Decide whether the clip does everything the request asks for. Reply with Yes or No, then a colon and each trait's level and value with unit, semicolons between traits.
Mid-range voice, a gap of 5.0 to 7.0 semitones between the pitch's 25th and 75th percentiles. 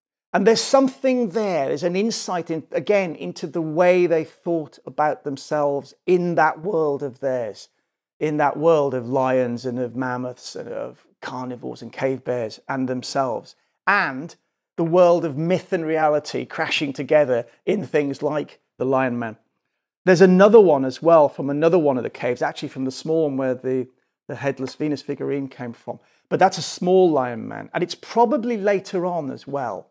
Yes: medium, 150 Hz; average, 5.3 semitones